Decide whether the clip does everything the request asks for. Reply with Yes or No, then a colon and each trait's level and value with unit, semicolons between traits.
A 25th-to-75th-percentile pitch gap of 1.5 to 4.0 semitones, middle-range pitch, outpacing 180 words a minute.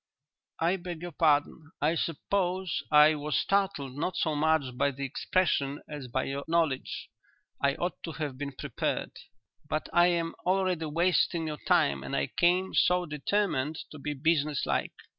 No: average, 3.6 semitones; medium, 155 Hz; average, 165 wpm